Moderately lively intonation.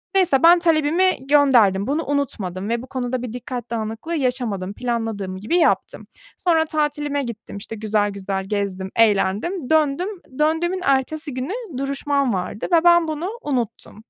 No: wide, 6.4 semitones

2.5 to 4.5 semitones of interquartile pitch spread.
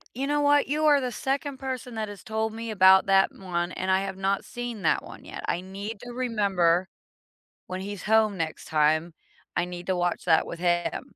No: average, 5.1 semitones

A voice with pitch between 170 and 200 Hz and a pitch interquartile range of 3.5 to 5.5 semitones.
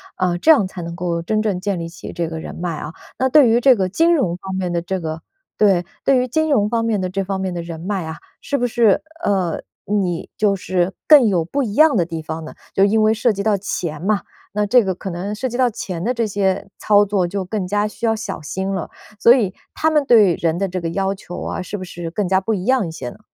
Yes: high, 195 Hz; average, 3.9 semitones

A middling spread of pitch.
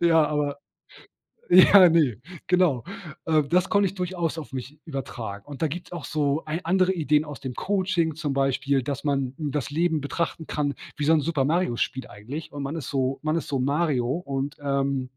Yes: average, 3.5 semitones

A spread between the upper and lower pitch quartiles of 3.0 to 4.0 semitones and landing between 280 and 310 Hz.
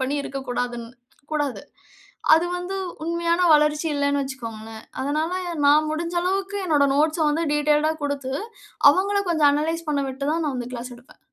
Yes: average, 3.6 semitones; very high, 295 Hz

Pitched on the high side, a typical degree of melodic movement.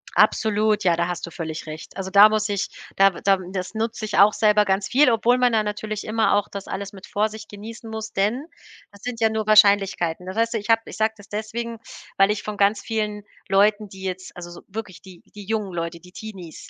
No: high, 205 Hz; narrow, 2.3 semitones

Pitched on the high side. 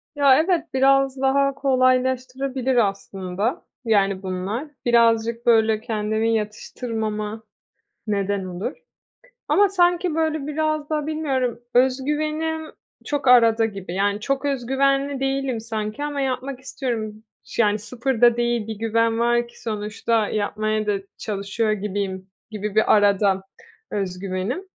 Yes: high, 235 Hz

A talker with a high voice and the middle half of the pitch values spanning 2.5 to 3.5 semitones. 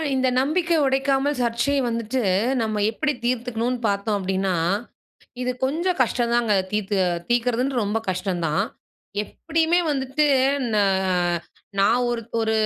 No: high, 240 Hz; average, 4.0 semitones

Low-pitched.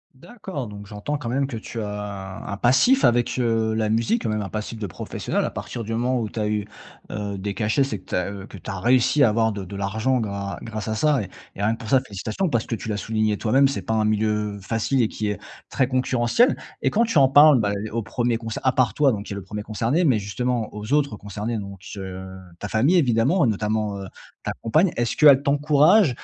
Yes: low, 110 Hz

